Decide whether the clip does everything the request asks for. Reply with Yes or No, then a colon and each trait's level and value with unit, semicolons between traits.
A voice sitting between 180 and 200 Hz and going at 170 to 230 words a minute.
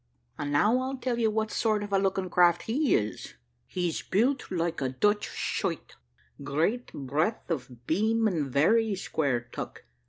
No: high, 190 Hz; average, 160 wpm